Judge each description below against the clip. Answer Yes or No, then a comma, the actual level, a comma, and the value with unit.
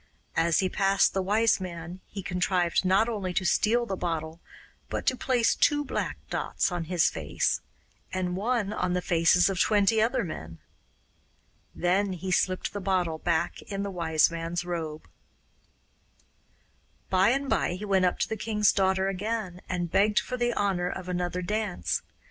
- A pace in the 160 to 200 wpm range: Yes, average, 165 wpm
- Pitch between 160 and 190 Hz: Yes, medium, 185 Hz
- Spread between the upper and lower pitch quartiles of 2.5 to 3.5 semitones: Yes, average, 2.9 semitones